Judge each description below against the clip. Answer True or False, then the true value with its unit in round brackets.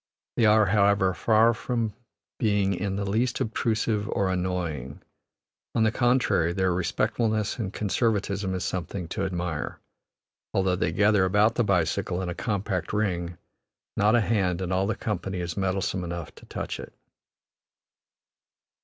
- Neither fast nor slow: True (145 wpm)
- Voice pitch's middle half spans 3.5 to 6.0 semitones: False (3.0 semitones)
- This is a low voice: True (100 Hz)